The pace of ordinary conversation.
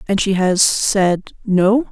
Yes: average, 155 wpm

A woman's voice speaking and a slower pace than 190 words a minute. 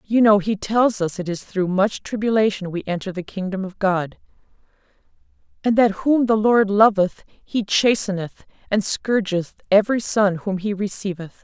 Yes: female; average, 165 wpm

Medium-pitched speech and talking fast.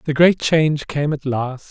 Yes: medium, 145 Hz; fast, 210 wpm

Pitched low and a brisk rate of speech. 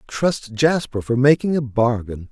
No: low, 130 Hz; average, 155 wpm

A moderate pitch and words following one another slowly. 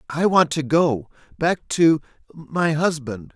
Yes: medium, 155 Hz; slow, 105 wpm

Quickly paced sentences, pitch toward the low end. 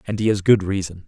Yes: fast, 280 wpm; low, 100 Hz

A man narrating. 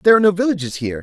Yes: male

